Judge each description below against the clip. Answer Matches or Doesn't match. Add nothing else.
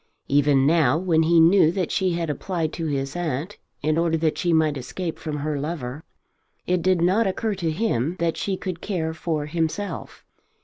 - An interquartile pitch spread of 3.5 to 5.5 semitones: Doesn't match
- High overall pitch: Doesn't match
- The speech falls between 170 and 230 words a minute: Matches